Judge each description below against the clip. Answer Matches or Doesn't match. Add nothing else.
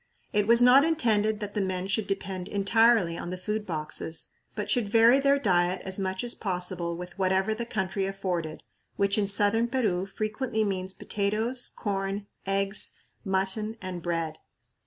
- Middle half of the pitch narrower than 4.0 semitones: Matches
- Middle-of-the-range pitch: Doesn't match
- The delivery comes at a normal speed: Matches